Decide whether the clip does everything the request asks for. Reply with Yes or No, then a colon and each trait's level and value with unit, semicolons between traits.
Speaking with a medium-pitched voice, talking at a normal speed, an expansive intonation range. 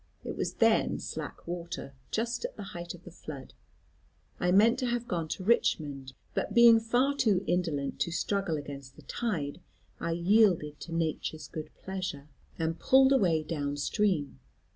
Yes: medium, 175 Hz; average, 165 wpm; wide, 6.0 semitones